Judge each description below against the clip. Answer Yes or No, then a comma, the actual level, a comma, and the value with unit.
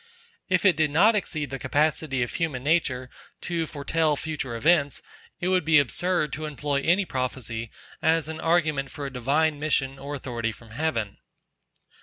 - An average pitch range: Yes, average, 3.3 semitones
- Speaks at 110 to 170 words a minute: Yes, average, 165 wpm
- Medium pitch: Yes, medium, 150 Hz